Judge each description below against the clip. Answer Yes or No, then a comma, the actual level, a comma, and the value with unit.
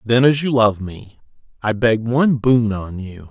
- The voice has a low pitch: Yes, low, 115 Hz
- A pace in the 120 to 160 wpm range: No, average, 200 wpm